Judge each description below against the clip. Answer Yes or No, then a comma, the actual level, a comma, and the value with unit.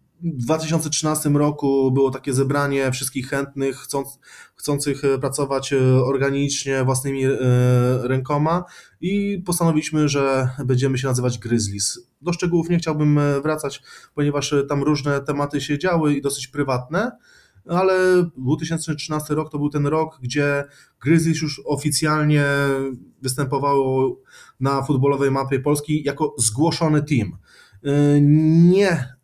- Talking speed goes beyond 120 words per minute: No, average, 115 wpm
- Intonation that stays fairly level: Yes, narrow, 2.2 semitones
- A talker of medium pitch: Yes, medium, 145 Hz